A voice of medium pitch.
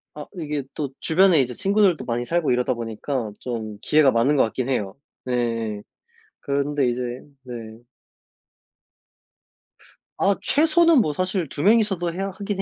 Yes: medium, 145 Hz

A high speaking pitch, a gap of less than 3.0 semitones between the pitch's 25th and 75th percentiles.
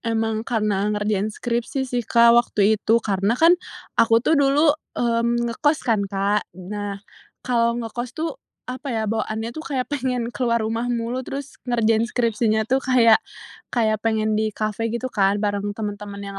Yes: high, 230 Hz; narrow, 2.4 semitones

